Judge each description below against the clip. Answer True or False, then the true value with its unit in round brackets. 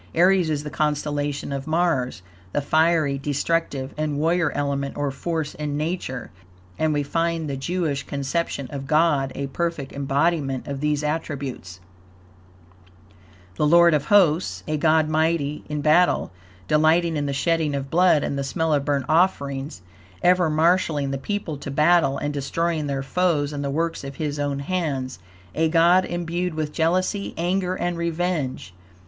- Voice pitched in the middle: True (150 Hz)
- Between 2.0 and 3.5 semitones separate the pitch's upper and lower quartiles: True (3.1 semitones)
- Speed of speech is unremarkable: True (155 wpm)